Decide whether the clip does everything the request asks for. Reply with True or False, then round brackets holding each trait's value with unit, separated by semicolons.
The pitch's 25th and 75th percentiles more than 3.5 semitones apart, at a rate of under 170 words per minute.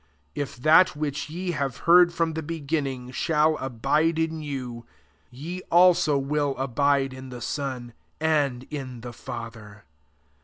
True (4.0 semitones; 140 wpm)